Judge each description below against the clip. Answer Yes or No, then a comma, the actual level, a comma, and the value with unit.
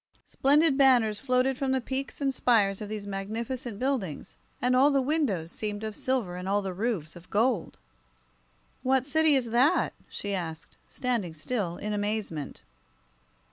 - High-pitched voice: Yes, high, 230 Hz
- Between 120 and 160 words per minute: Yes, average, 155 wpm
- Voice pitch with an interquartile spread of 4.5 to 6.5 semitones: Yes, average, 5.0 semitones